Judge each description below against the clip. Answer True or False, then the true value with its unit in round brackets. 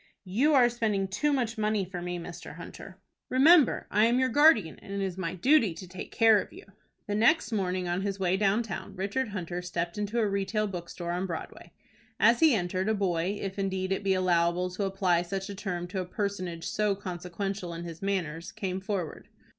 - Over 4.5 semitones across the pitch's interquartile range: False (3.0 semitones)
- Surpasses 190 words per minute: True (205 wpm)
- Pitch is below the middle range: False (195 Hz)